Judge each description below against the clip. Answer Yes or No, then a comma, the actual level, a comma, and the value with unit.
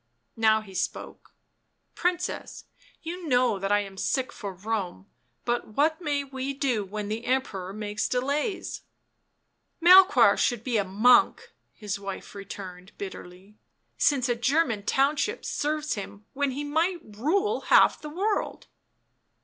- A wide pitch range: Yes, wide, 6.7 semitones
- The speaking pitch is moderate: No, high, 245 Hz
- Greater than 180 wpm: No, average, 150 wpm